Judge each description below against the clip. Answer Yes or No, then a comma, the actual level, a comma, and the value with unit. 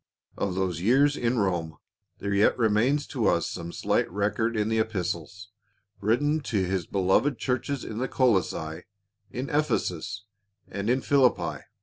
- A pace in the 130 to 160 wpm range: Yes, average, 140 wpm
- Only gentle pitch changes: No, average, 5.1 semitones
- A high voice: No, low, 105 Hz